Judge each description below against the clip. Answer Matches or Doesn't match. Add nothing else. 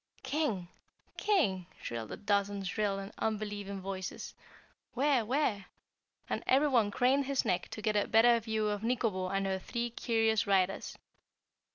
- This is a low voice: Doesn't match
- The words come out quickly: Doesn't match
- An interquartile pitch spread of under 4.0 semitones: Matches